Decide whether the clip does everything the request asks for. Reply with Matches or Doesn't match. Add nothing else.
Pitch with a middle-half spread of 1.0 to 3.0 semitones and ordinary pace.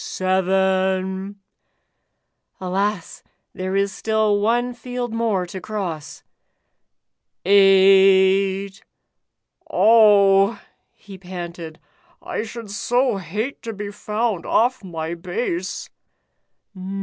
Doesn't match